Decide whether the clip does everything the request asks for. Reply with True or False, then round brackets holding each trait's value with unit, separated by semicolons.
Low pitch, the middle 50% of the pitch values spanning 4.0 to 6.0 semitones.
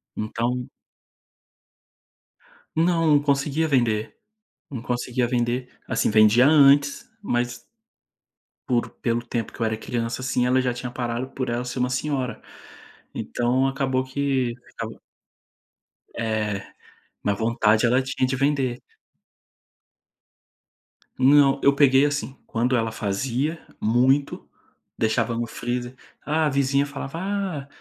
False (125 Hz; 2.8 semitones)